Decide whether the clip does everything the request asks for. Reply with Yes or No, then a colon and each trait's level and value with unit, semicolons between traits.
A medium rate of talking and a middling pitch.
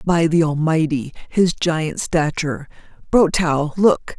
No: slow, 85 wpm; medium, 160 Hz